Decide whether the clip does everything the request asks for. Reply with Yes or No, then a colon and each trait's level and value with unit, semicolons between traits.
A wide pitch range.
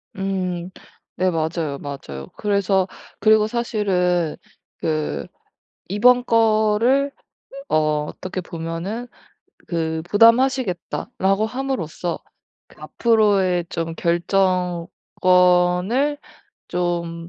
No: average, 4.3 semitones